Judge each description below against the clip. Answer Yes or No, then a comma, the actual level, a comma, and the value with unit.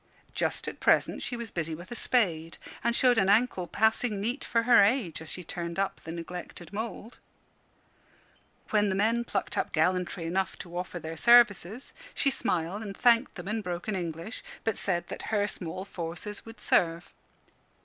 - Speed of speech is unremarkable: Yes, average, 175 wpm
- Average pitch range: Yes, average, 4.6 semitones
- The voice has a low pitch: No, high, 195 Hz